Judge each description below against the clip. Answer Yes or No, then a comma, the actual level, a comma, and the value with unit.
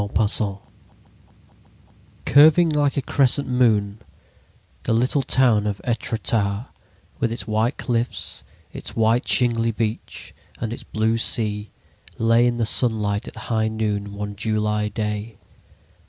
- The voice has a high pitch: No, low, 110 Hz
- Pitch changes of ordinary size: No, narrow, 2.2 semitones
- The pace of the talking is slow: Yes, slow, 125 wpm